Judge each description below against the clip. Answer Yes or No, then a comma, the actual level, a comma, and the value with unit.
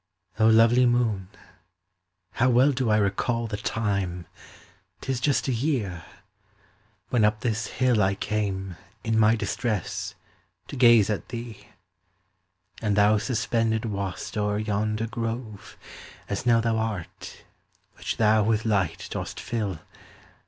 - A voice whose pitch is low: Yes, low, 110 Hz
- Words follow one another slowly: Yes, slow, 125 wpm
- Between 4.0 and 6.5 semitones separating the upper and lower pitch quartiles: No, narrow, 2.4 semitones